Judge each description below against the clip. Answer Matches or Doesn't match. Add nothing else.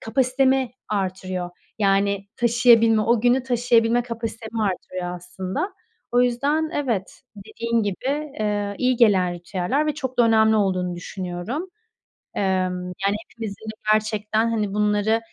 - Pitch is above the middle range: Matches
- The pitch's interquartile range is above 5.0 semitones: Doesn't match